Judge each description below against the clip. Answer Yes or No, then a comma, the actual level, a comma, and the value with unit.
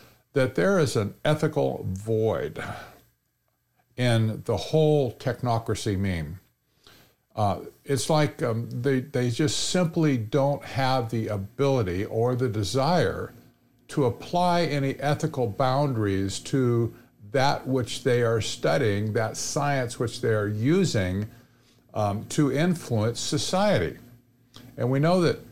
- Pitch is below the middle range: Yes, low, 125 Hz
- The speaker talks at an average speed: No, slow, 120 wpm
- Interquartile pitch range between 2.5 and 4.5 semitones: Yes, average, 4.0 semitones